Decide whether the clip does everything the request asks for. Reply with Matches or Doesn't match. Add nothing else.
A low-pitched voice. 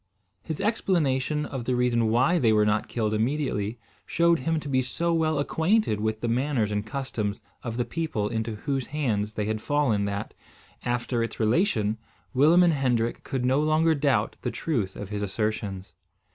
Matches